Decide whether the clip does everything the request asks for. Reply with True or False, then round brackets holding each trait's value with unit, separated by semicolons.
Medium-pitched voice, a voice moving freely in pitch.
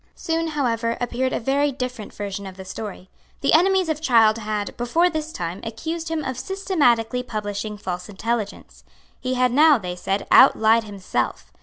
False (235 Hz; 6.1 semitones)